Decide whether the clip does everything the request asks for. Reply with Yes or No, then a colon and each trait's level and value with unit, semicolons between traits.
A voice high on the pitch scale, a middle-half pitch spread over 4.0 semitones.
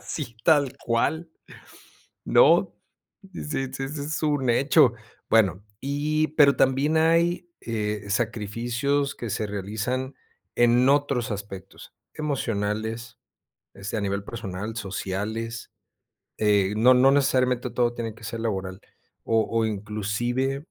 No: low, 120 Hz; average, 4.6 semitones